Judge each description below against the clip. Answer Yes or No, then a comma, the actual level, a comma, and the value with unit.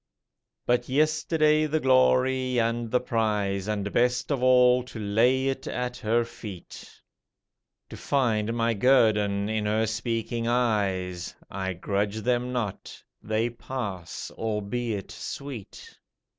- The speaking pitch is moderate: No, low, 115 Hz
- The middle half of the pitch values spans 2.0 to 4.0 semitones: Yes, average, 3.2 semitones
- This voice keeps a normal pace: No, slow, 120 wpm